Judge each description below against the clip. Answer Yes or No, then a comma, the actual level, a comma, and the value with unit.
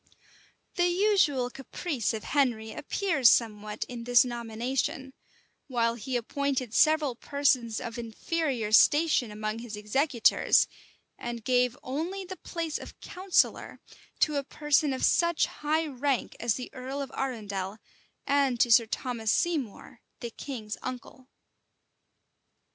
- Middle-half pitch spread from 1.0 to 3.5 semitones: No, average, 4.1 semitones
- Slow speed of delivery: Yes, slow, 130 wpm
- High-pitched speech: Yes, very high, 255 Hz